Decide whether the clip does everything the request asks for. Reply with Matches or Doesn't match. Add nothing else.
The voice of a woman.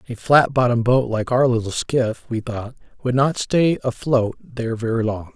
Doesn't match